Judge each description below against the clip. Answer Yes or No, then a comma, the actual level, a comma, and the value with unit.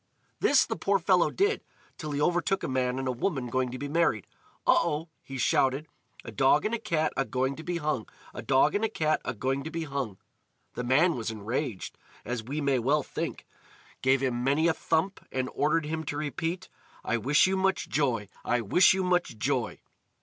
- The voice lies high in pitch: No, medium, 145 Hz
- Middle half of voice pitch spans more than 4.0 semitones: Yes, average, 4.6 semitones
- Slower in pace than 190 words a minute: No, average, 200 wpm